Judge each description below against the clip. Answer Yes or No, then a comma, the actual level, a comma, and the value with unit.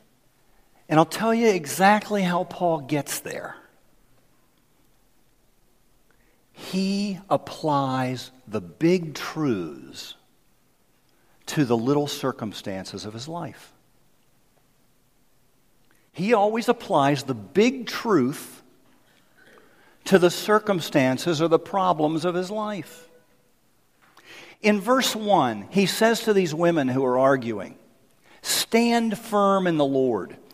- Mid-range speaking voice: Yes, medium, 170 Hz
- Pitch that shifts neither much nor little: No, wide, 6.6 semitones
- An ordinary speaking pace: No, slow, 100 wpm